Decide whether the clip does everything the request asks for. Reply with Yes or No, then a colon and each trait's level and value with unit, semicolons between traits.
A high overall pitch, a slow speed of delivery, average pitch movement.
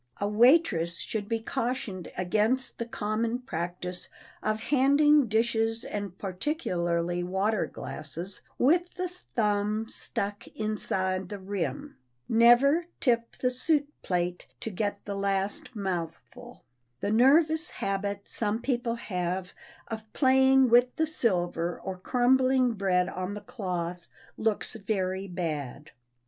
Yes: high, 215 Hz; slow, 120 wpm; average, 5.0 semitones